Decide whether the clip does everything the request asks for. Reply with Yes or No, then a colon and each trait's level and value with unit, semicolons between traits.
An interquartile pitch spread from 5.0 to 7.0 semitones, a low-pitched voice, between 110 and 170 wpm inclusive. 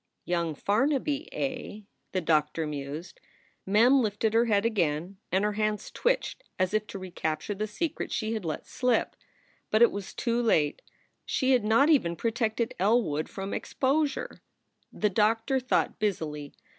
No: average, 5.3 semitones; high, 215 Hz; average, 150 wpm